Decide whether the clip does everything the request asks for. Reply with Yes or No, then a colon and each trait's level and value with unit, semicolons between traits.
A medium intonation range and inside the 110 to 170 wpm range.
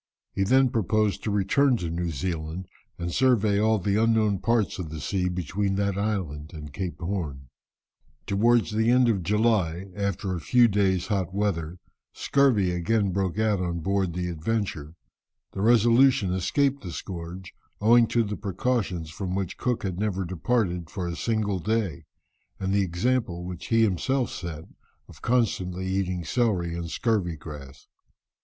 Yes: average, 4.0 semitones; average, 155 wpm